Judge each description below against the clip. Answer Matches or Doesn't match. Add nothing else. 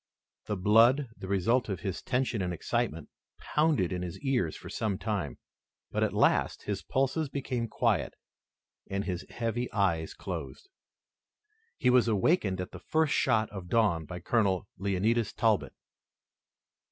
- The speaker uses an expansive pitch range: Doesn't match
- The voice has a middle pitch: Doesn't match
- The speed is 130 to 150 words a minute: Matches